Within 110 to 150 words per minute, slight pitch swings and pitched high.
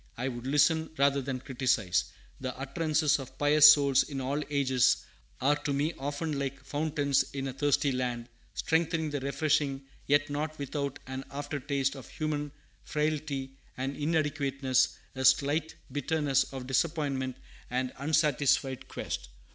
No: average, 140 wpm; narrow, 2.0 semitones; medium, 140 Hz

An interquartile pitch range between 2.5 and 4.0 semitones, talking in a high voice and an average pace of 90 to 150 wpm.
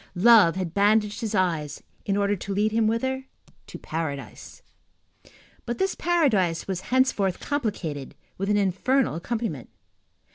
No: average, 4.8 semitones; high, 205 Hz; slow, 135 wpm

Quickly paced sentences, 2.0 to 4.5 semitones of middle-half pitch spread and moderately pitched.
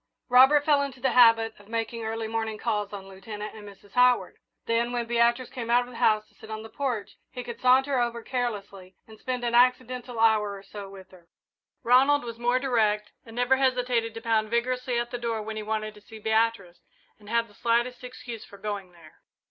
No: fast, 210 wpm; narrow, 2.6 semitones; high, 230 Hz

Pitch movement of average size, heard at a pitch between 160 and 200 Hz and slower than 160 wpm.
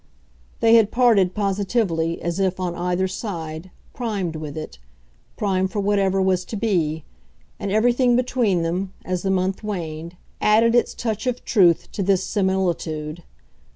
Yes: average, 3.6 semitones; high, 190 Hz; average, 150 wpm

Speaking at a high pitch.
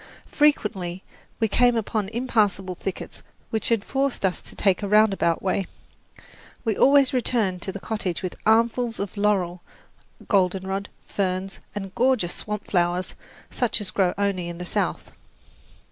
Yes: high, 200 Hz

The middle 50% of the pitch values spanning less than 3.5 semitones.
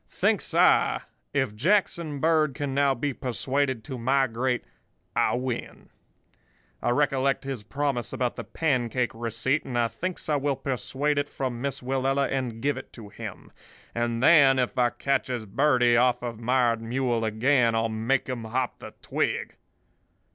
Yes: average, 2.8 semitones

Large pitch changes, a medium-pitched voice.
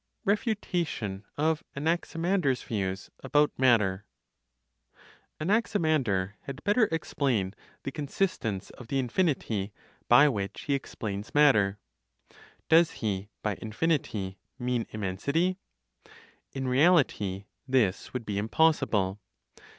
No: wide, 7.7 semitones; low, 130 Hz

